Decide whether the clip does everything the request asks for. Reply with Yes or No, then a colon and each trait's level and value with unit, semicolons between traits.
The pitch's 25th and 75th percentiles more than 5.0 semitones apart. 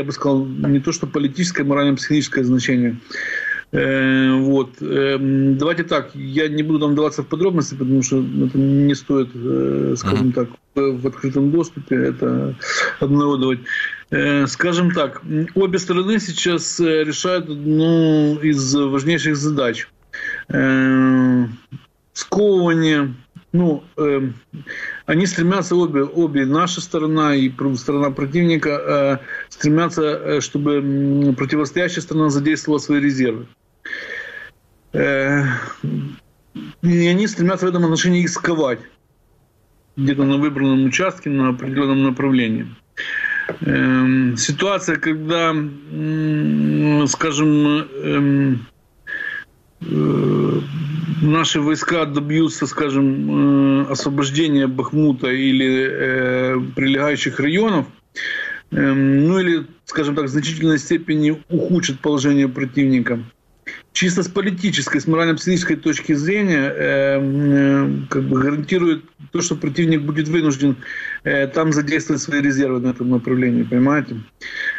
No: average, 3.3 semitones